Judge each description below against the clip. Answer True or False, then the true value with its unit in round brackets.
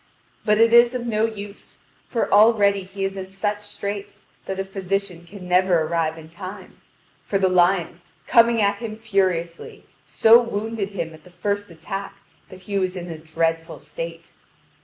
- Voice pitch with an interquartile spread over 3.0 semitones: False (2.7 semitones)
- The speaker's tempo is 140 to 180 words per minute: True (170 wpm)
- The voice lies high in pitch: True (195 Hz)